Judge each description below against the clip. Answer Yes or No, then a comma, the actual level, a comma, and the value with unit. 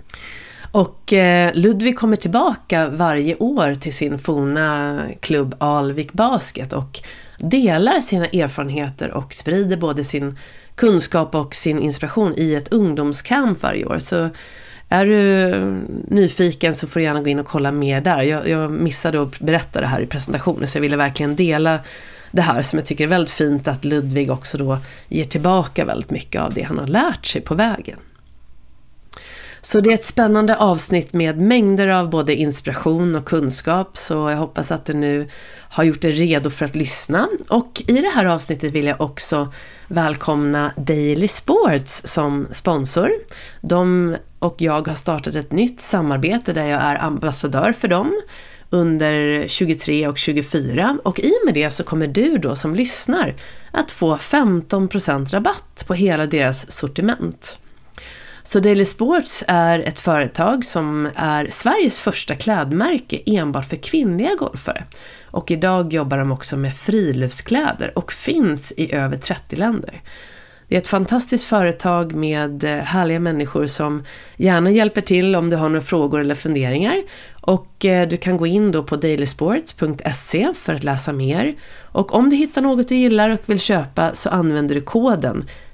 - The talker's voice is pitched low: No, medium, 160 Hz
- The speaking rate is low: No, average, 160 wpm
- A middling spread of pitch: Yes, average, 4.8 semitones